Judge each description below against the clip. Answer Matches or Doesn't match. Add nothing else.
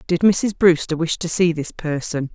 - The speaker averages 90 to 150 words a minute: Doesn't match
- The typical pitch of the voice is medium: Matches